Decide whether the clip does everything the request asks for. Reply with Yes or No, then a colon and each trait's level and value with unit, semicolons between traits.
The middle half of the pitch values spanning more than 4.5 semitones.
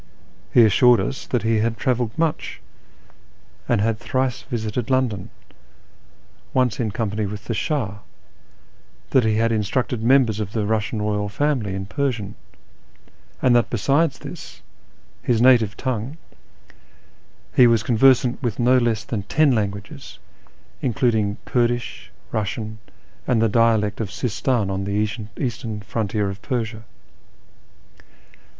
No: average, 3.0 semitones